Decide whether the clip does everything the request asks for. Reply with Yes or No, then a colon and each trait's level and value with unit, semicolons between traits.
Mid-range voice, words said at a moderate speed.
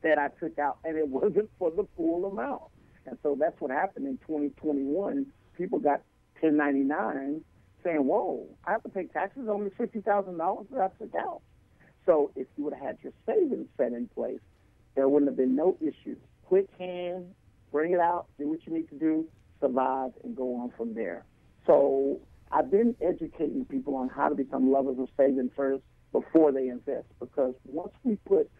Yes: medium, 160 Hz; average, 185 wpm